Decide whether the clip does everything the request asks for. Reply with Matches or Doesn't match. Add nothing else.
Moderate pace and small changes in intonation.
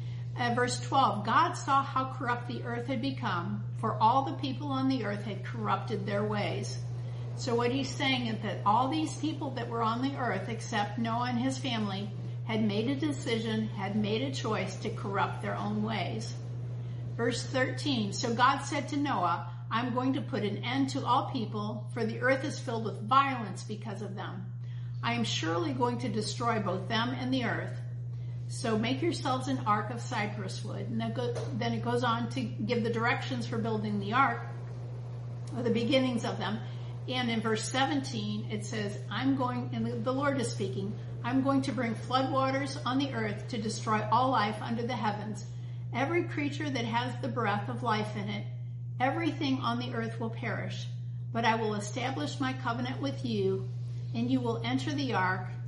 Matches